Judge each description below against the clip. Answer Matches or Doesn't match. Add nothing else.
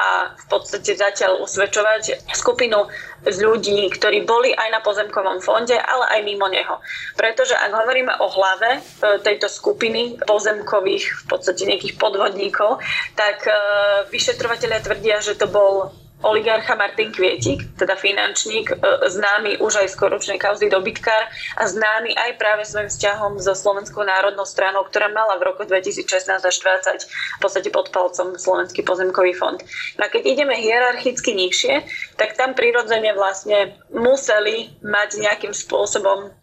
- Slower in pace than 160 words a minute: Matches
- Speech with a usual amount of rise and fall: Matches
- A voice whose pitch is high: Matches